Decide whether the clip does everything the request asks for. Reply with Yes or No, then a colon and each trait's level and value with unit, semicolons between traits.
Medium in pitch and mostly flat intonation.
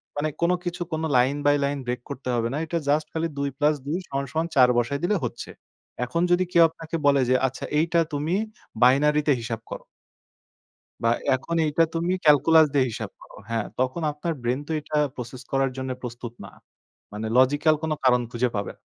No: medium, 145 Hz; average, 4.1 semitones